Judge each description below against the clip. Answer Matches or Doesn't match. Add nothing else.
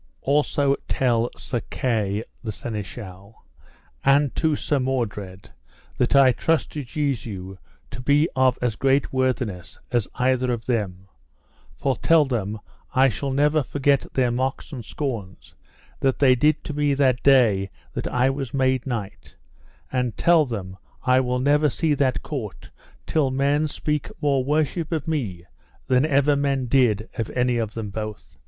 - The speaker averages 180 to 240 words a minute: Doesn't match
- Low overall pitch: Matches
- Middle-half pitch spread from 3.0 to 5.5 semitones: Matches